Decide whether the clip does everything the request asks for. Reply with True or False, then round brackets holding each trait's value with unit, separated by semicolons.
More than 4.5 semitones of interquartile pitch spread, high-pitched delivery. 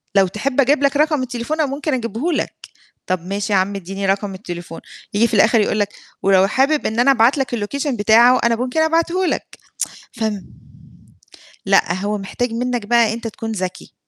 True (5.1 semitones; 230 Hz)